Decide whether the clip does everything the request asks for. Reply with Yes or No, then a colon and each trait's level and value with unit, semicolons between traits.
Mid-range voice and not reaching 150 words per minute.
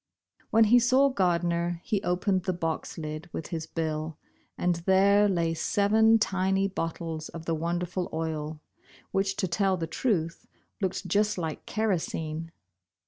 Yes: medium, 175 Hz; average, 140 wpm